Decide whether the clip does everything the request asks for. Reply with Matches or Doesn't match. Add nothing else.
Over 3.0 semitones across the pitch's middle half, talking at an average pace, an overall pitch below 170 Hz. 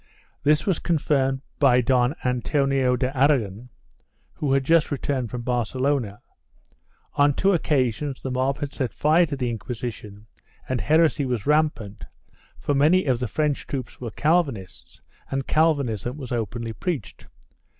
Matches